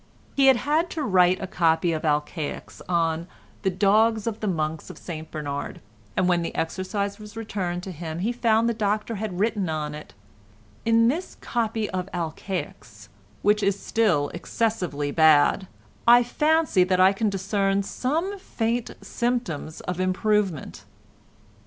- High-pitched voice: Yes, high, 195 Hz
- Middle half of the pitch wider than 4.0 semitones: Yes, average, 5.2 semitones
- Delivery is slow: No, average, 145 wpm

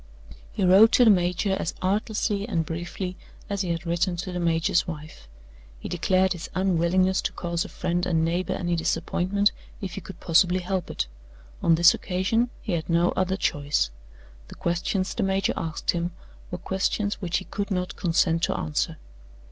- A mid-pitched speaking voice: Yes, medium, 180 Hz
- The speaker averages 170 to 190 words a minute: Yes, average, 180 wpm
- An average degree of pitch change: No, narrow, 2.2 semitones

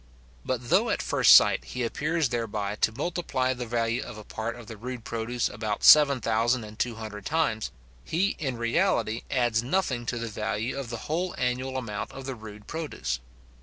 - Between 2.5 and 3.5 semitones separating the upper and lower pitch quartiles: Yes, average, 3.0 semitones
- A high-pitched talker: No, low, 120 Hz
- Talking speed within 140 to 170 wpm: No, average, 190 wpm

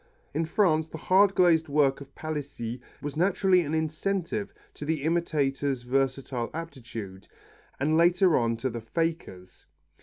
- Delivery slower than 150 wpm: Yes, average, 140 wpm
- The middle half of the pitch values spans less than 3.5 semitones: No, average, 4.1 semitones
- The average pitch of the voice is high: No, medium, 155 Hz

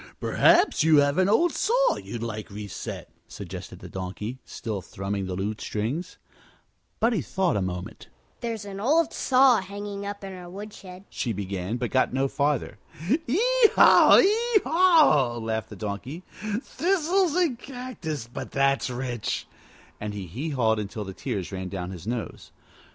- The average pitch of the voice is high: No, medium, 140 Hz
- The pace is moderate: Yes, average, 155 wpm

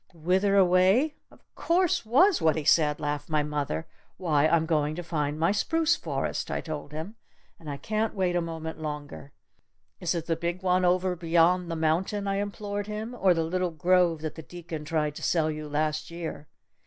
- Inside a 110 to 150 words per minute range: No, average, 190 wpm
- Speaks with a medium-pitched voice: Yes, medium, 170 Hz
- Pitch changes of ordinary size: Yes, average, 3.4 semitones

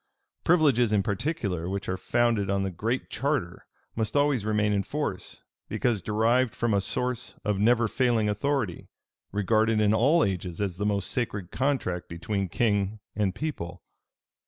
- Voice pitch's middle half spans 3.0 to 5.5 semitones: Yes, average, 3.7 semitones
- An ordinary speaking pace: Yes, average, 155 wpm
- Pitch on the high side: No, low, 105 Hz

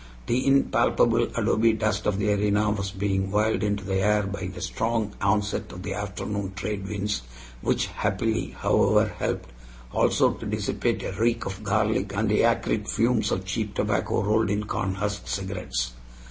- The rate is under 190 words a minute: Yes, average, 160 wpm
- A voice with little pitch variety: Yes, narrow, 1.7 semitones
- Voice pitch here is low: Yes, low, 105 Hz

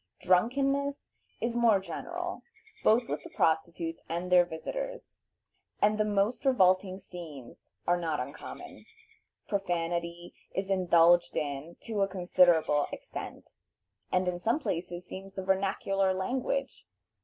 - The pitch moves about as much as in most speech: Yes, average, 3.7 semitones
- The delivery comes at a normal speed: No, slow, 120 wpm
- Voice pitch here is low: No, medium, 185 Hz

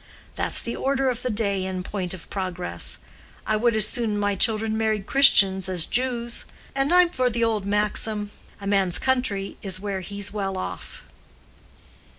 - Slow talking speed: No, average, 165 wpm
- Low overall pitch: No, high, 210 Hz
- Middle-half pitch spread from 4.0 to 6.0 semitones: No, average, 3.4 semitones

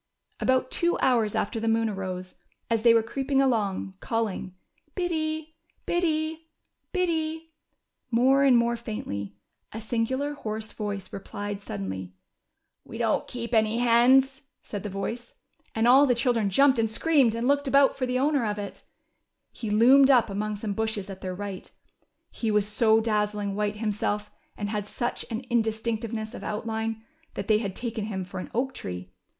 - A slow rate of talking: No, average, 165 wpm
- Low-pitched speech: No, high, 225 Hz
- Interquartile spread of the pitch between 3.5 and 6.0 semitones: Yes, average, 3.9 semitones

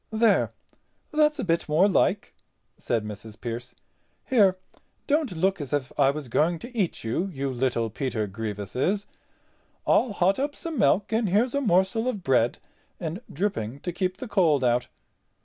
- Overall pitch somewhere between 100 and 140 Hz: No, medium, 175 Hz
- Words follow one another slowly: No, average, 165 wpm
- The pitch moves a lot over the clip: Yes, wide, 8.6 semitones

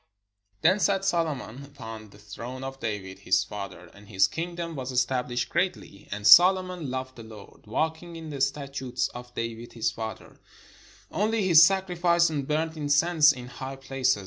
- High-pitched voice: No, low, 135 Hz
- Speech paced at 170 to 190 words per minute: No, average, 160 wpm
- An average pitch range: No, wide, 6.4 semitones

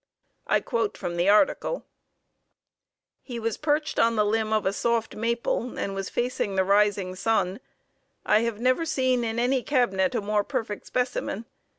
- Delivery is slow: No, average, 165 wpm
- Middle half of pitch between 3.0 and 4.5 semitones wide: Yes, average, 3.3 semitones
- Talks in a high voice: Yes, high, 225 Hz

